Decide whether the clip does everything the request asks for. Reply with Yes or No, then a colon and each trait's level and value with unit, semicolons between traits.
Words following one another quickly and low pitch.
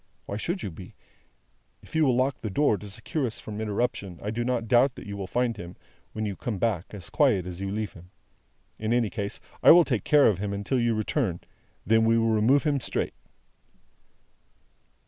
Yes: fast, 210 wpm; low, 110 Hz